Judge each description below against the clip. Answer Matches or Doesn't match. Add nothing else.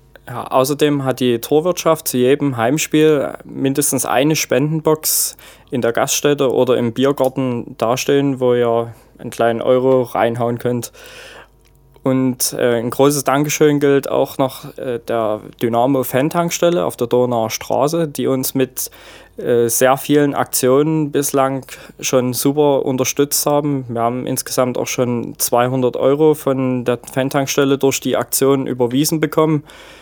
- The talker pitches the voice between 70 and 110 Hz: Doesn't match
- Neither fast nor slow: Matches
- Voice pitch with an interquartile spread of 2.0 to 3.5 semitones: Matches